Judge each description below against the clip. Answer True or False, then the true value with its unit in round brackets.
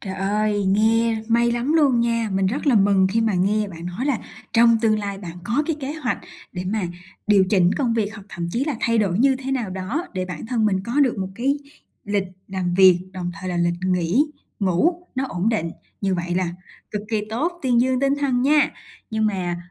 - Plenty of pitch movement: False (4.6 semitones)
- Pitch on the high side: True (215 Hz)